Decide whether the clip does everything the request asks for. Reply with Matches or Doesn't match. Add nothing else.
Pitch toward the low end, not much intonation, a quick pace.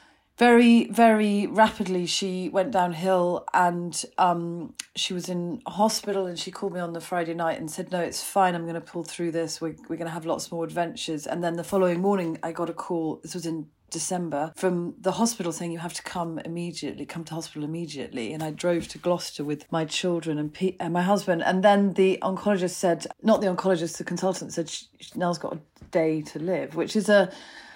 Doesn't match